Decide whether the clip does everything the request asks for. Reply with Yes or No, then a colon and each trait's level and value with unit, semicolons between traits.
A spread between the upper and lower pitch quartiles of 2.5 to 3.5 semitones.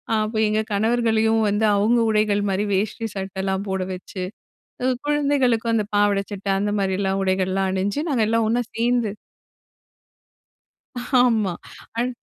Yes: average, 2.8 semitones